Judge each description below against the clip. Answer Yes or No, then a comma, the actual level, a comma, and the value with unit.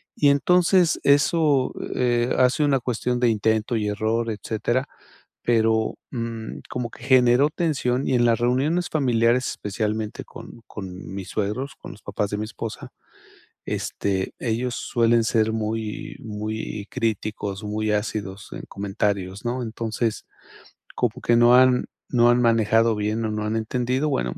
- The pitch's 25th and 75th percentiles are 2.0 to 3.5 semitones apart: Yes, average, 2.8 semitones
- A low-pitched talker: Yes, low, 115 Hz